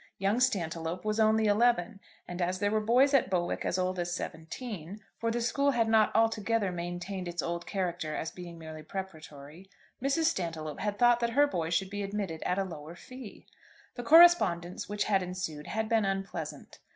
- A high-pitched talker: Yes, high, 195 Hz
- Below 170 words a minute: No, average, 185 wpm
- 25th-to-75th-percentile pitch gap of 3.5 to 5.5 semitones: Yes, average, 4.5 semitones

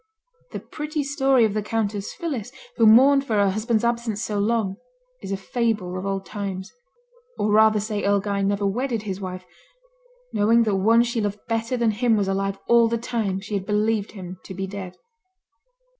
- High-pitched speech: Yes, high, 210 Hz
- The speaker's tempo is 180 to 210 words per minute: Yes, average, 190 wpm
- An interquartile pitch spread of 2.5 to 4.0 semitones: Yes, average, 2.8 semitones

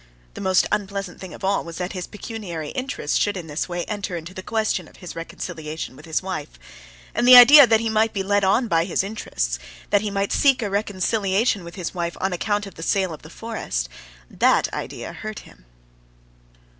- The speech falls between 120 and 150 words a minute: No, fast, 205 wpm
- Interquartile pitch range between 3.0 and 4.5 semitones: Yes, average, 3.8 semitones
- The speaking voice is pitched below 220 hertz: Yes, high, 190 Hz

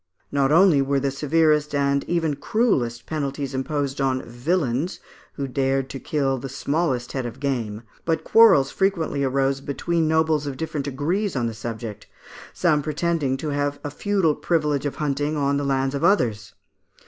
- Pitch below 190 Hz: Yes, medium, 140 Hz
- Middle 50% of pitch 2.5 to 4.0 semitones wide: Yes, average, 2.8 semitones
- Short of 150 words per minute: No, average, 170 wpm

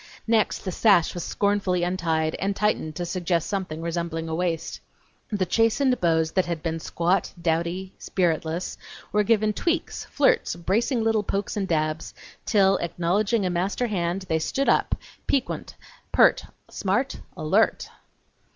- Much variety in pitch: No, average, 3.7 semitones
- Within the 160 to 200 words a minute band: No, average, 140 wpm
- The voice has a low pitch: No, medium, 180 Hz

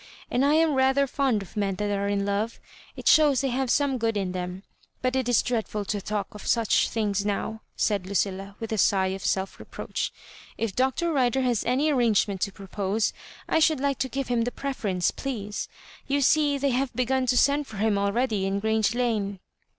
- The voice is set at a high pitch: Yes, high, 225 Hz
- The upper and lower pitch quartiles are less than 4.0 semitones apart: No, average, 4.7 semitones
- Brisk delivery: Yes, fast, 210 wpm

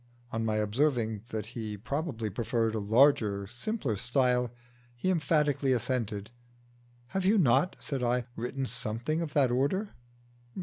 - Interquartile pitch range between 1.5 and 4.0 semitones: No, average, 4.4 semitones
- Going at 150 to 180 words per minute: No, slow, 135 wpm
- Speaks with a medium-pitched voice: No, low, 125 Hz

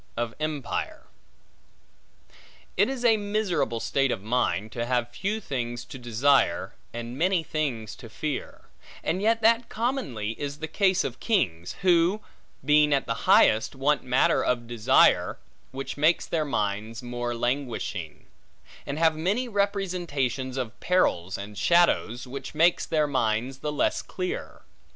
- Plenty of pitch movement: Yes, wide, 6.9 semitones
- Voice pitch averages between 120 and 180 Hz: Yes, medium, 140 Hz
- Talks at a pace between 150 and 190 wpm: No, average, 140 wpm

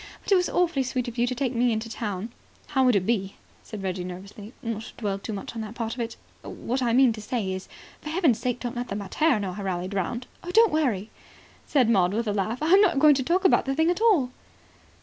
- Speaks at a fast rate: Yes, fast, 250 wpm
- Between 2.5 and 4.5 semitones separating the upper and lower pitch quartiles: No, average, 4.9 semitones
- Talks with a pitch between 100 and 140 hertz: No, high, 235 Hz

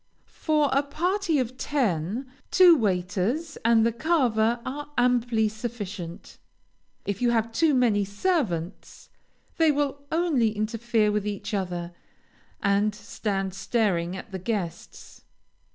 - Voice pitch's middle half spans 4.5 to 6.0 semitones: Yes, wide, 5.5 semitones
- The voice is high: Yes, high, 225 Hz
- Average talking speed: No, slow, 120 wpm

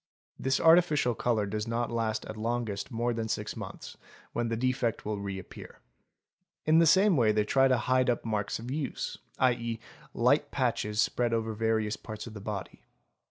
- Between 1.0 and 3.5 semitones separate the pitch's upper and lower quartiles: Yes, average, 2.9 semitones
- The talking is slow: No, average, 175 wpm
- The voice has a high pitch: No, low, 115 Hz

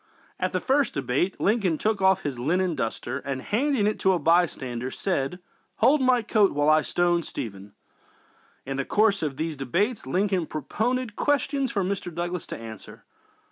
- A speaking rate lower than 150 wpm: No, average, 180 wpm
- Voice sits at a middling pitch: Yes, medium, 180 Hz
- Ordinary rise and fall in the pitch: No, wide, 7.2 semitones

